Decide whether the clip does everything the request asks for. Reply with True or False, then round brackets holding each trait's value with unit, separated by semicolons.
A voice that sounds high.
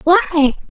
True (320 Hz)